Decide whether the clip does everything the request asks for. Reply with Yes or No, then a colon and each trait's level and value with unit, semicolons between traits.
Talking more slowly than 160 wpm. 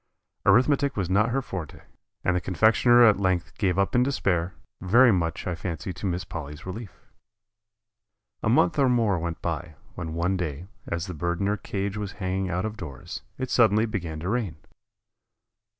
No: average, 180 wpm